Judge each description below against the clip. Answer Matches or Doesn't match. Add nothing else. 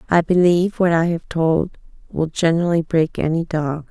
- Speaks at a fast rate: Doesn't match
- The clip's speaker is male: Doesn't match